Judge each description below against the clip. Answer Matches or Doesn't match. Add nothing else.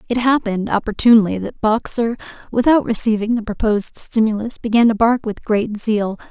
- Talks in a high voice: Matches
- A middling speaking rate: Matches